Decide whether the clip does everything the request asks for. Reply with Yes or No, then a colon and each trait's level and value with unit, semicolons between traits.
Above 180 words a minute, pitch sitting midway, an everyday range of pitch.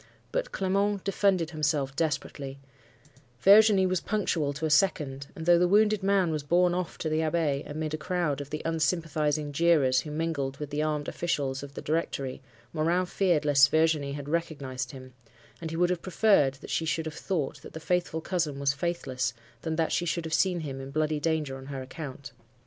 Yes: average, 195 wpm; medium, 155 Hz; average, 3.5 semitones